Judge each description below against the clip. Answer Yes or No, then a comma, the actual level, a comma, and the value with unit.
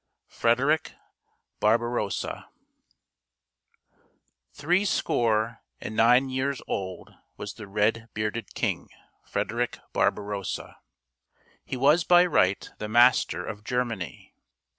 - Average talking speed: No, slow, 95 wpm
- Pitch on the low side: Yes, low, 115 Hz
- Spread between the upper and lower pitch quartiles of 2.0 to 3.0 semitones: No, average, 3.6 semitones